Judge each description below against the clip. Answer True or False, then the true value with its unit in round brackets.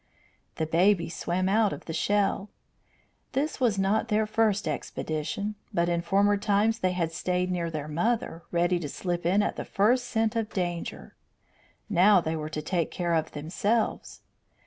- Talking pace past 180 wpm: False (170 wpm)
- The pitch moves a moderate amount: True (3.7 semitones)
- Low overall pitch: False (185 Hz)